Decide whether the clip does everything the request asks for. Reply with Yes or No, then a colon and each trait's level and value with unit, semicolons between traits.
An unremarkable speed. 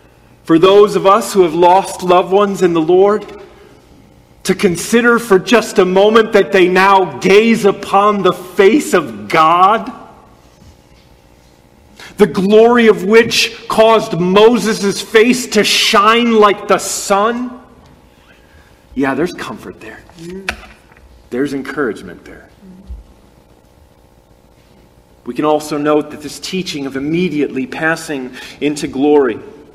No: slow, 115 wpm